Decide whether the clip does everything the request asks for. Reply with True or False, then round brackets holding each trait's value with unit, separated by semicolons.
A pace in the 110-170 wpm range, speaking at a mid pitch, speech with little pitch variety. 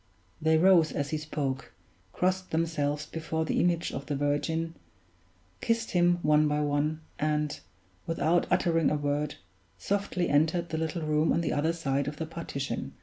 True (160 wpm; 155 Hz; 2.3 semitones)